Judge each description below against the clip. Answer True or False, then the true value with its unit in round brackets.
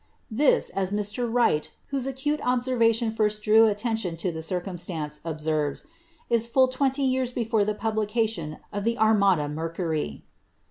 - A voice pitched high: True (215 Hz)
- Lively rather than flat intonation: True (6.0 semitones)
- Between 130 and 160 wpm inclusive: True (150 wpm)